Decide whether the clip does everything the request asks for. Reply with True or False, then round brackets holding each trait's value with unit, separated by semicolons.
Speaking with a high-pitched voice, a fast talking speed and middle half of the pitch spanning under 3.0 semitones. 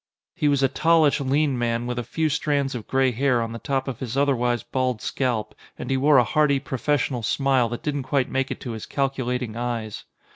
False (130 Hz; 215 wpm; 2.6 semitones)